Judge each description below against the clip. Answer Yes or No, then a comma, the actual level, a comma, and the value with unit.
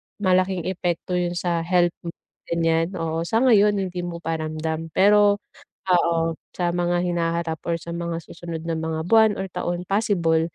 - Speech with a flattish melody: Yes, narrow, 2.0 semitones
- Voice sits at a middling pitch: Yes, medium, 175 Hz